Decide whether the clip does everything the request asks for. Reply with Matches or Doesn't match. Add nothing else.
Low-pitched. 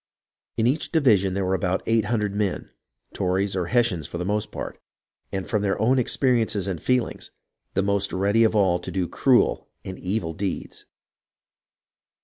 Matches